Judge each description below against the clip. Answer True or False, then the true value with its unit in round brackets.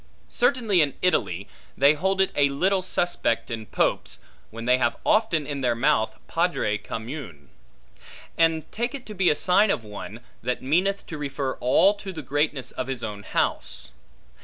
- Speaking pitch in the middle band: True (145 Hz)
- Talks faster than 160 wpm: True (170 wpm)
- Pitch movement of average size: False (7.4 semitones)